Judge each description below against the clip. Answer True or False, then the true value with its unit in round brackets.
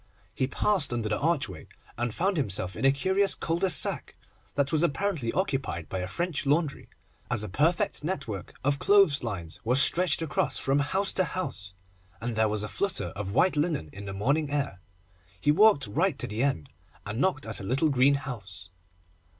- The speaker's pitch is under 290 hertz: True (140 Hz)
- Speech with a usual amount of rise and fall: False (7.8 semitones)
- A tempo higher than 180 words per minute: True (190 wpm)